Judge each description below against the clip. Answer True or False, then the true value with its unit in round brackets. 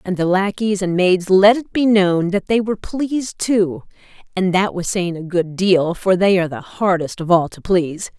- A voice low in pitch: False (190 Hz)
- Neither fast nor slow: False (220 wpm)